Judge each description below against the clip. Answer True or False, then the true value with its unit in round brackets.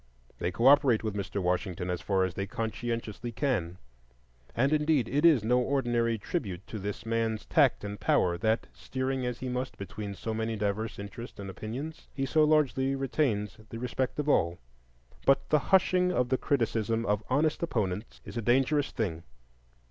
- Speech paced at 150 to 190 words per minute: True (170 wpm)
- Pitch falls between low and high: False (115 Hz)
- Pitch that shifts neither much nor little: True (4.7 semitones)